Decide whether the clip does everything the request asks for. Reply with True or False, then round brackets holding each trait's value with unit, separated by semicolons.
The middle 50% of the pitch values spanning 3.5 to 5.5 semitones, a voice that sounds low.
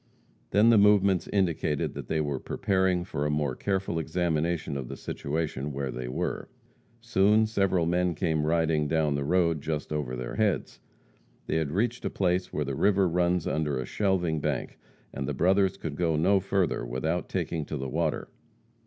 True (4.1 semitones; 80 Hz)